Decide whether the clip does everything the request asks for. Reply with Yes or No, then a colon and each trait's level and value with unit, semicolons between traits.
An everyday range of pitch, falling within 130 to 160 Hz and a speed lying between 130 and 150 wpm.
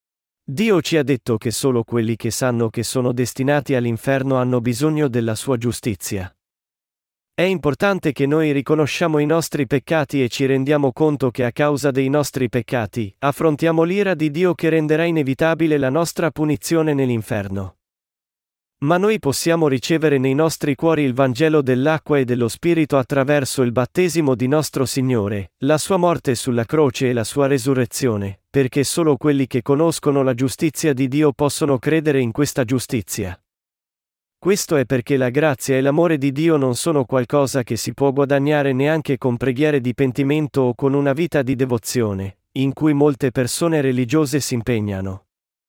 No: average, 3.5 semitones; medium, 140 Hz; average, 160 wpm